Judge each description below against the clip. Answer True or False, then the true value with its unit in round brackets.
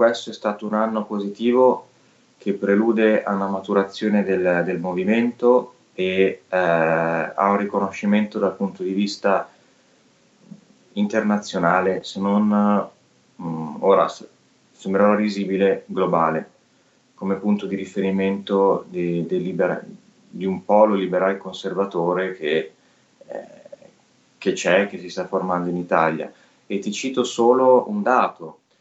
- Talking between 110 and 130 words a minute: True (125 wpm)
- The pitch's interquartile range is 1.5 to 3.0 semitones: True (2.4 semitones)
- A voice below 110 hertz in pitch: True (100 Hz)